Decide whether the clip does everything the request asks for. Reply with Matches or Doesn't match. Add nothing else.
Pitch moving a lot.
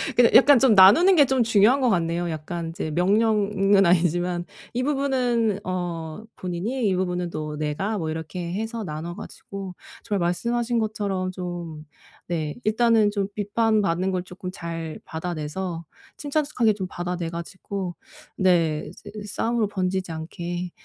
Doesn't match